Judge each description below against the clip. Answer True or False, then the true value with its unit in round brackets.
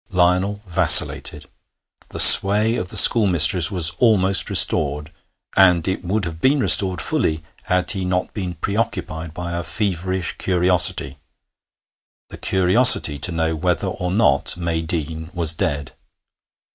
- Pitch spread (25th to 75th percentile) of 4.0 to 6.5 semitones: False (2.9 semitones)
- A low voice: True (90 Hz)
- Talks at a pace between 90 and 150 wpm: True (135 wpm)